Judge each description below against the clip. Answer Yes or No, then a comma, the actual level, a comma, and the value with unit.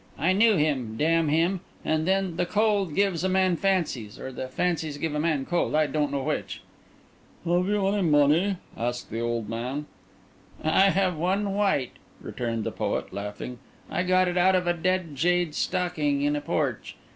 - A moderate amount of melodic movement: Yes, average, 4.5 semitones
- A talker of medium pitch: Yes, medium, 165 Hz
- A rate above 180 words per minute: No, average, 175 wpm